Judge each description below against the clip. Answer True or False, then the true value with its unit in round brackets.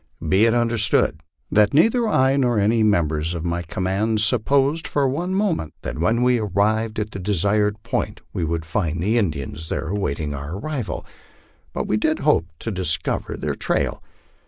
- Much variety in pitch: True (5.8 semitones)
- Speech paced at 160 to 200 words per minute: True (170 wpm)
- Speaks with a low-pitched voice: True (105 Hz)